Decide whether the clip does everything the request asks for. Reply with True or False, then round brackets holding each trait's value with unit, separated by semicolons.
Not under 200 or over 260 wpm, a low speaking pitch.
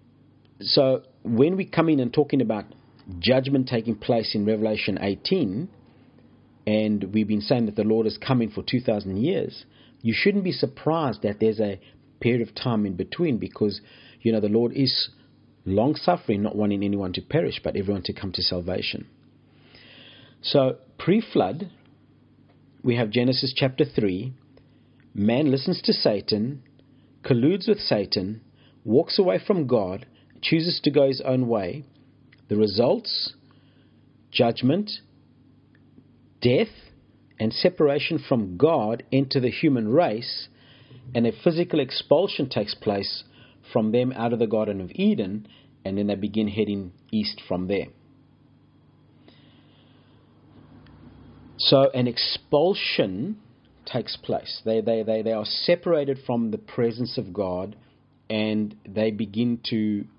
False (135 wpm; 125 Hz)